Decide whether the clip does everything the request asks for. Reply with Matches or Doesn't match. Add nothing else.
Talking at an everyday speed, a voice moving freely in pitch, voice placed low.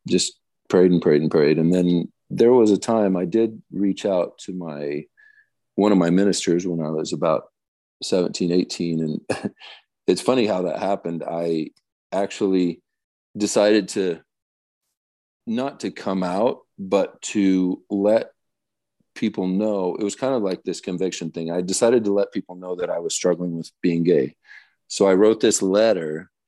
Doesn't match